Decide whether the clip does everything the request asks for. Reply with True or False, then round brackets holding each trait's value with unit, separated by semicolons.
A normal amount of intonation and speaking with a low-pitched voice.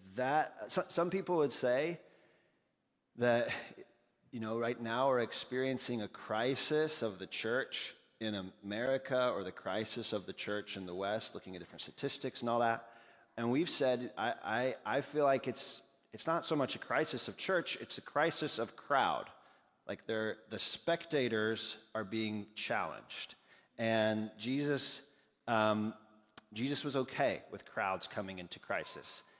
True (3.9 semitones; 115 Hz)